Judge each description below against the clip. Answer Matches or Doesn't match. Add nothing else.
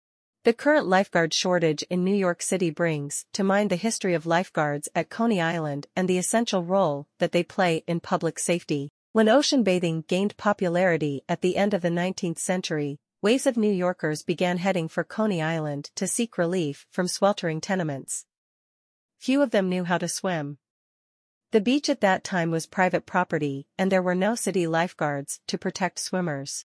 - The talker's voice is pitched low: Doesn't match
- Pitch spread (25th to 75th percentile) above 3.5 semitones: Doesn't match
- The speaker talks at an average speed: Matches